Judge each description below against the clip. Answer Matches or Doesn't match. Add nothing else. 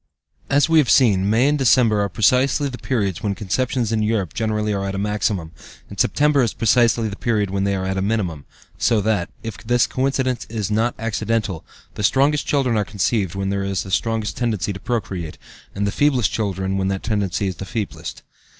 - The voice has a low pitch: Matches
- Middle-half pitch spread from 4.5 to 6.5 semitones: Doesn't match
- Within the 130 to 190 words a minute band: Doesn't match